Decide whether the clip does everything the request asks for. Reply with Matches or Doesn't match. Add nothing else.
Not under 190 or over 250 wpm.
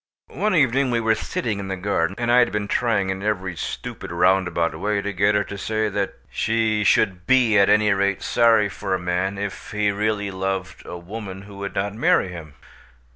Matches